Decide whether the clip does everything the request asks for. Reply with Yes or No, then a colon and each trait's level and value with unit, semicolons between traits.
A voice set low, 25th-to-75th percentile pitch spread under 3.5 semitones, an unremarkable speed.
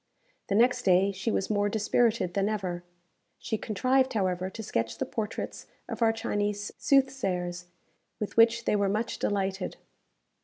No: high, 205 Hz; average, 3.1 semitones; average, 150 wpm